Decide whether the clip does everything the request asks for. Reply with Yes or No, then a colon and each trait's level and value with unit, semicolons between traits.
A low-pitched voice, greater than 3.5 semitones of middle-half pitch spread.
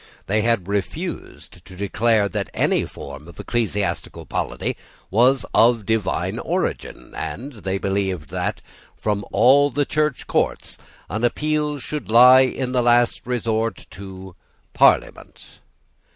Yes: low, 115 Hz; average, 4.1 semitones